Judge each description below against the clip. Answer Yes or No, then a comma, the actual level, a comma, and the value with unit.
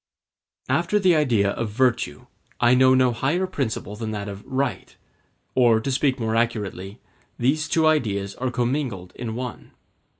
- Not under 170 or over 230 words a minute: No, average, 155 wpm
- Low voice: Yes, low, 120 Hz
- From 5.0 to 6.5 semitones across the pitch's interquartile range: No, average, 3.7 semitones